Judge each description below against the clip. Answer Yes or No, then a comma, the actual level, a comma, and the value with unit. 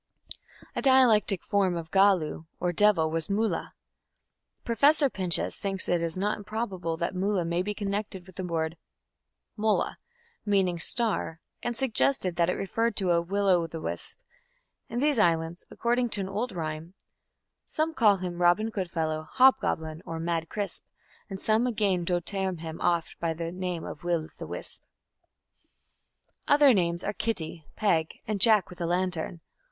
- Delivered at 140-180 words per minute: Yes, average, 160 wpm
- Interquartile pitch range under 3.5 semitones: No, average, 3.9 semitones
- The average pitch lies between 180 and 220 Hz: Yes, medium, 185 Hz